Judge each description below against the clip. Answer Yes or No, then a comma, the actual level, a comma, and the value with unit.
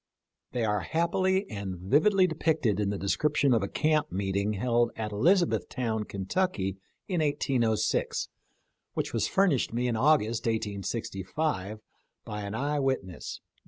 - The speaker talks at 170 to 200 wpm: No, average, 140 wpm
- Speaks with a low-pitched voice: Yes, low, 115 Hz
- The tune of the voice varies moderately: No, wide, 7.0 semitones